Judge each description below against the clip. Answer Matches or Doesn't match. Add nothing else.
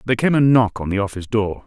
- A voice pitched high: Doesn't match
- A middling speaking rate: Doesn't match